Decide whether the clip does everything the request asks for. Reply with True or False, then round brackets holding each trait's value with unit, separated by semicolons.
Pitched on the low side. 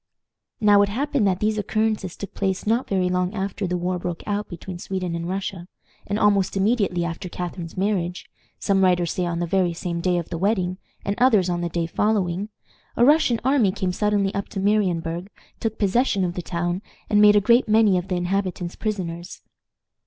False (190 Hz)